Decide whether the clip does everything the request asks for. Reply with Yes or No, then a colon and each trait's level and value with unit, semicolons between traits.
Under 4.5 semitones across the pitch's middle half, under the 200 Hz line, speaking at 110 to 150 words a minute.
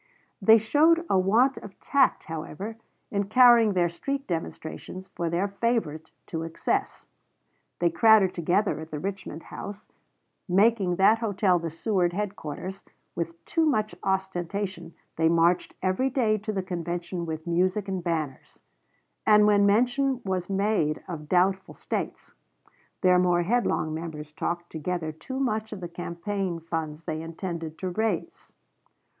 Yes: average, 4.0 semitones; medium, 185 Hz; average, 140 wpm